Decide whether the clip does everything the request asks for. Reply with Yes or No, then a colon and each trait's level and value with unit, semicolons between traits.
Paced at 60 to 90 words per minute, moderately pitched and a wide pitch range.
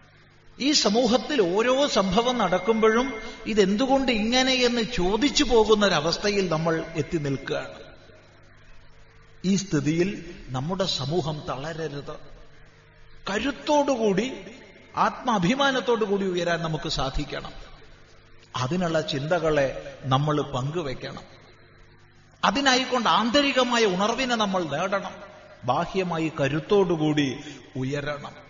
Yes: average, 75 wpm; medium, 170 Hz; wide, 7.5 semitones